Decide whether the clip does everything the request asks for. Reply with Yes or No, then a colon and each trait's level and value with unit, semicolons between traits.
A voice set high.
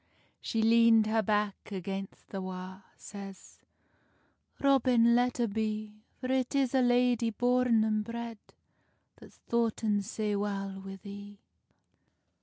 Yes: high, 220 Hz